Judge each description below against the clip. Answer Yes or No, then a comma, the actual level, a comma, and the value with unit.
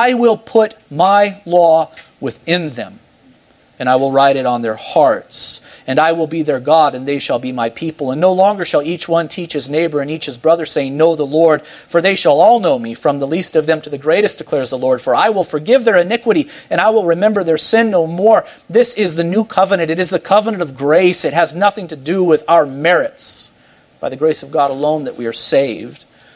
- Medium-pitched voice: Yes, medium, 165 Hz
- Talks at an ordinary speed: No, fast, 235 wpm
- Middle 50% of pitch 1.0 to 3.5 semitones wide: No, average, 4.2 semitones